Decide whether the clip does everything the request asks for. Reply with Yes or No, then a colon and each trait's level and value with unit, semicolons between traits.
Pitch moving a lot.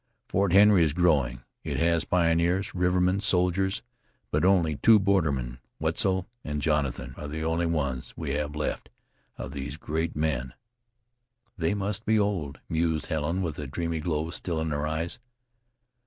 No: average, 3.3 semitones